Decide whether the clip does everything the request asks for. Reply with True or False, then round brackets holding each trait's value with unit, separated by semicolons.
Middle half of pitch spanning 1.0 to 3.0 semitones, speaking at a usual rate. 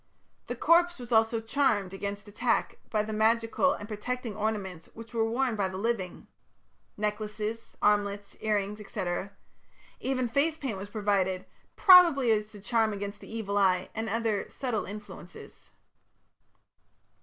True (2.5 semitones; 145 wpm)